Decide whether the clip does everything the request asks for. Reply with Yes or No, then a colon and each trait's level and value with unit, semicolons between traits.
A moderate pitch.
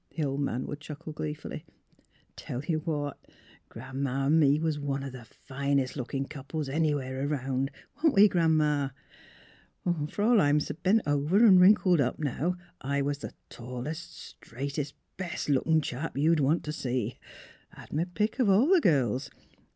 Yes: medium, 145 Hz